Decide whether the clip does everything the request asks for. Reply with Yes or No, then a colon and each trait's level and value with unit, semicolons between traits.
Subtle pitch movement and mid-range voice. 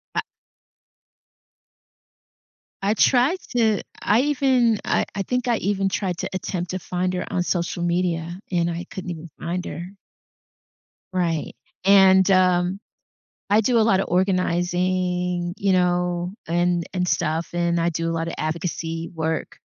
Yes: narrow, 2.1 semitones; medium, 180 Hz